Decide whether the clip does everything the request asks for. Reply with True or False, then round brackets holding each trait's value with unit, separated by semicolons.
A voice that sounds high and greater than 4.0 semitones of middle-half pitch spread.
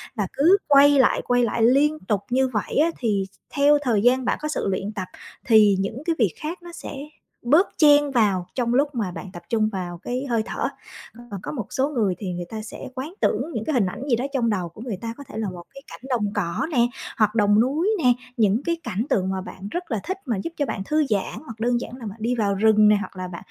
True (230 Hz; 5.2 semitones)